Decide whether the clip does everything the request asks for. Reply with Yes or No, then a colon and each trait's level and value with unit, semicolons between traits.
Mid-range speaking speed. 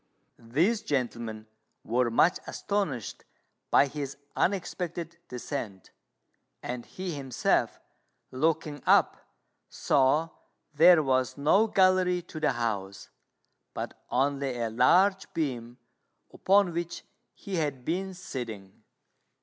No: slow, 100 wpm